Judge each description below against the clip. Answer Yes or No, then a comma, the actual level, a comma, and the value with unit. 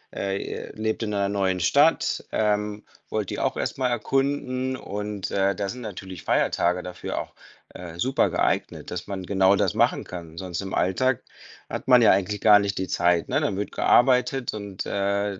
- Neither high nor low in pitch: No, low, 100 Hz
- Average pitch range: Yes, average, 3.0 semitones